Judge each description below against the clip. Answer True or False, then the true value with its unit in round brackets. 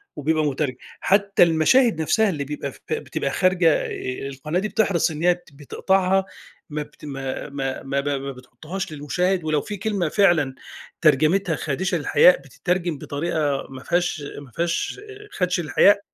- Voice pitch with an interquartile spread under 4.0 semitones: False (4.7 semitones)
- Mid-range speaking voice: True (160 Hz)